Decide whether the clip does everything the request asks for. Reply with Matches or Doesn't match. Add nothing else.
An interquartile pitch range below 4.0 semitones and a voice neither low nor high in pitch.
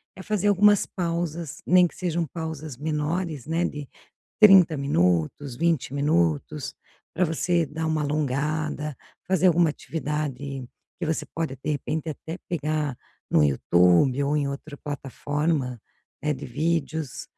Matches